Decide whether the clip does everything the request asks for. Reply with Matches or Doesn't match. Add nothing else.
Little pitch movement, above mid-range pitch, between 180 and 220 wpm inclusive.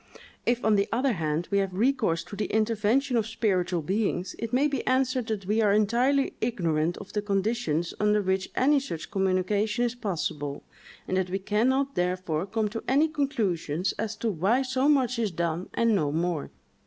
Doesn't match